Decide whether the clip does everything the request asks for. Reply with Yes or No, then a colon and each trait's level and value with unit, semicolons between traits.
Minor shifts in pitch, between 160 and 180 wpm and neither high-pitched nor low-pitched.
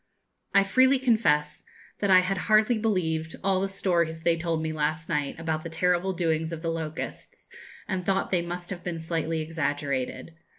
No: average, 3.1 semitones; average, 175 wpm; medium, 170 Hz